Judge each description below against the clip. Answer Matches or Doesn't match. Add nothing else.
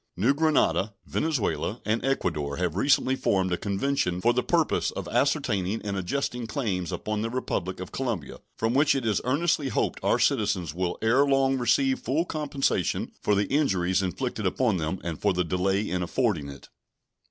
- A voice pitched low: Matches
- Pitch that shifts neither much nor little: Doesn't match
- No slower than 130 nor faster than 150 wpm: Doesn't match